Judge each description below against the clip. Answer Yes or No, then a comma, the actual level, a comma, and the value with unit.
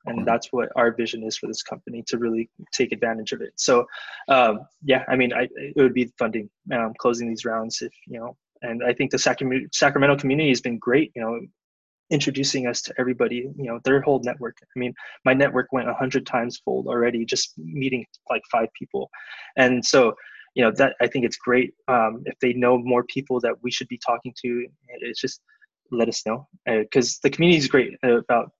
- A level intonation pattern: Yes, narrow, 2.3 semitones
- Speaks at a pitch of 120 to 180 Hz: Yes, low, 125 Hz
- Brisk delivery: Yes, fast, 210 wpm